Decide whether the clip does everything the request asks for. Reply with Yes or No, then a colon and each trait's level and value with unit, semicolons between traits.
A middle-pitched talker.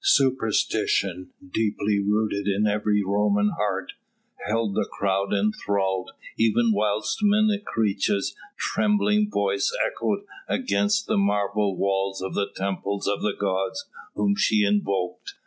No: low, 105 Hz